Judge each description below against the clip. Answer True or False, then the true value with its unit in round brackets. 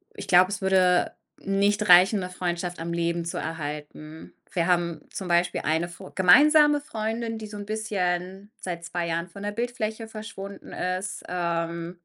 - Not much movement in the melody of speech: False (3.3 semitones)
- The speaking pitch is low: False (180 Hz)